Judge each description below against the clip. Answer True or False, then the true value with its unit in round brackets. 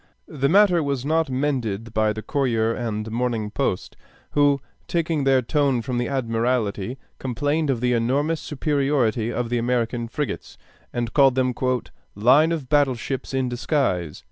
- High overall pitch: False (125 Hz)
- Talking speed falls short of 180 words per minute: True (150 wpm)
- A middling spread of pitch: True (3.8 semitones)